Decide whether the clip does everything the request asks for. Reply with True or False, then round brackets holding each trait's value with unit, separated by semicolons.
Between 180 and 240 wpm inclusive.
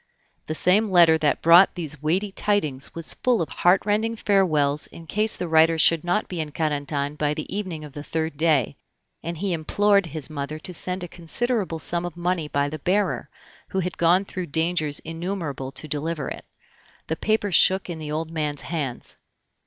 True (185 wpm)